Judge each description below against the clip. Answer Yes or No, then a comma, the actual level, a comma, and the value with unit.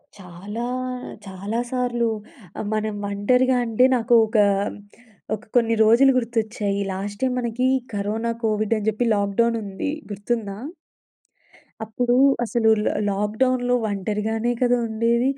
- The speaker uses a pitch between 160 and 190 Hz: No, high, 225 Hz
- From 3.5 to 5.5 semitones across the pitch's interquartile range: No, average, 2.8 semitones